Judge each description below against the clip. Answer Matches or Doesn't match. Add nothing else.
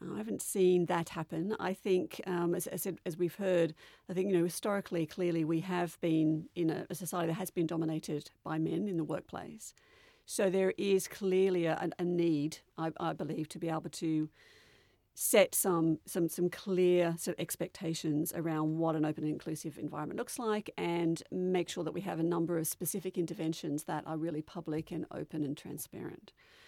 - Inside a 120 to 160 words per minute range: Doesn't match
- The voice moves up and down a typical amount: Doesn't match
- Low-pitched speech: Doesn't match